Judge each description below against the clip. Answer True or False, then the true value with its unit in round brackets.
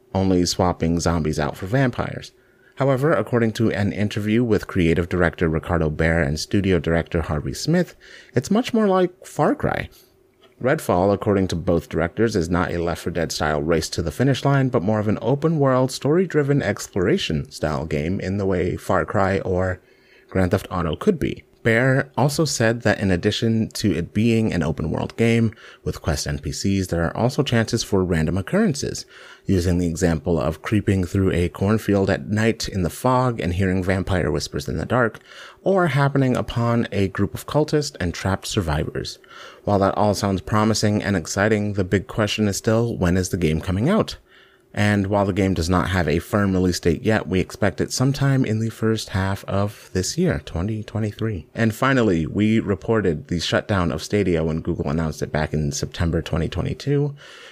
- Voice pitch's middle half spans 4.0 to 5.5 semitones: True (4.6 semitones)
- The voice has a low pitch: True (100 Hz)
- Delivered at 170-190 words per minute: True (185 wpm)